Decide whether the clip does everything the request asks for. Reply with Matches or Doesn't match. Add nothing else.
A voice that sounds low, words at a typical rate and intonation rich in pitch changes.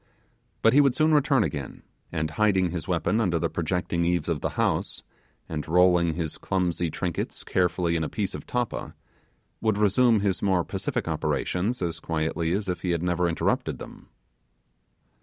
Doesn't match